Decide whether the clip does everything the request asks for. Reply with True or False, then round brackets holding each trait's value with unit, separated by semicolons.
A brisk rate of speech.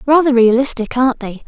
False (160 wpm)